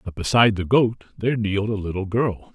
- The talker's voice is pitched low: Yes, low, 105 Hz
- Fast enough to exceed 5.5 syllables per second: Yes, 6.0 syllables/s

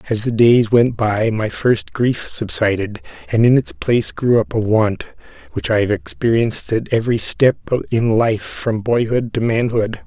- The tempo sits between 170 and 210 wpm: Yes, average, 180 wpm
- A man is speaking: Yes, male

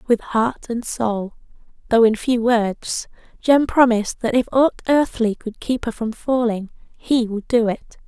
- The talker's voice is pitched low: No, high, 235 Hz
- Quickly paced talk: No, average, 170 wpm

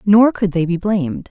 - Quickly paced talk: Yes, fast, 230 wpm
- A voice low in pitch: No, high, 190 Hz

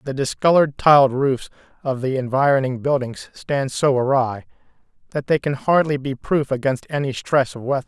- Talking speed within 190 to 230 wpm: No, average, 170 wpm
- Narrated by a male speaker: Yes, male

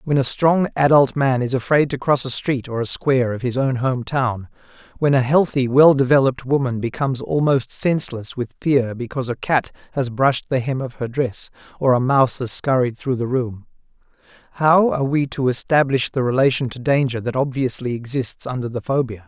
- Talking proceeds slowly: No, average, 190 wpm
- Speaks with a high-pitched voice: No, low, 130 Hz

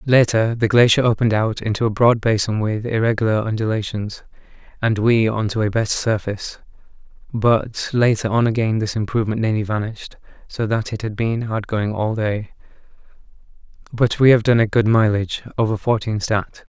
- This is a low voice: Yes, low, 110 Hz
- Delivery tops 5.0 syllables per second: Yes, 5.3 syllables/s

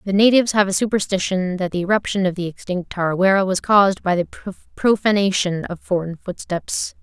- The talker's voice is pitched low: No, high, 190 Hz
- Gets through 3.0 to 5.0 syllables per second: No, 5.4 syllables/s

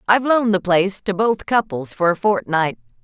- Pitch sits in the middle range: No, high, 195 Hz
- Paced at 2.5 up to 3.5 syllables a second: No, 5.7 syllables/s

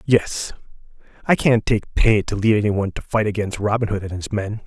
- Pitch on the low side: Yes, low, 105 Hz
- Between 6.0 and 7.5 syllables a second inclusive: No, 5.3 syllables/s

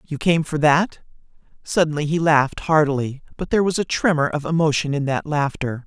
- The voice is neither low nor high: Yes, medium, 155 Hz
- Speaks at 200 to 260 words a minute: No, average, 185 wpm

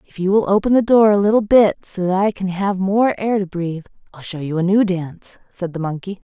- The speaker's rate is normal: No, fast, 255 wpm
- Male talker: No, female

